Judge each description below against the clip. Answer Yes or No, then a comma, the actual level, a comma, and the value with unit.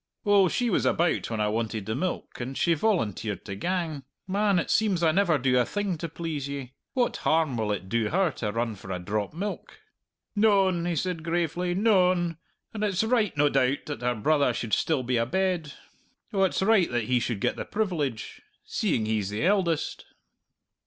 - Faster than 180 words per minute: Yes, average, 195 wpm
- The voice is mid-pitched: Yes, medium, 160 Hz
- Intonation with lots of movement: Yes, wide, 7.8 semitones